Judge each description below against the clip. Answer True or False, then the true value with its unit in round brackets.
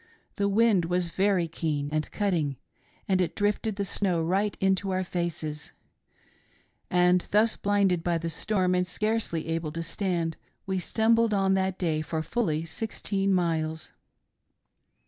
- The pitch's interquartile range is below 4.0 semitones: True (3.4 semitones)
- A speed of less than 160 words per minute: True (145 wpm)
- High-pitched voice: False (180 Hz)